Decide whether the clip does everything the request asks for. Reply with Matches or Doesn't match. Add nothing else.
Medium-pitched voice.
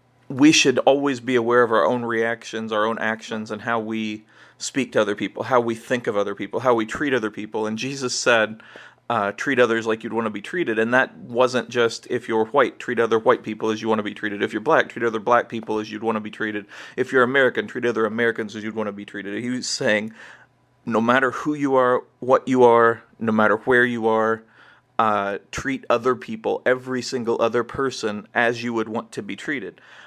Doesn't match